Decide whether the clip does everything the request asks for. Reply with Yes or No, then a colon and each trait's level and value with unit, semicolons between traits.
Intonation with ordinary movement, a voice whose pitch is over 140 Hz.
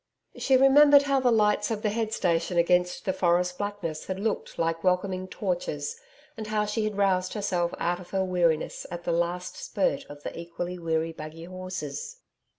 Yes: average, 3.8 semitones; medium, 185 Hz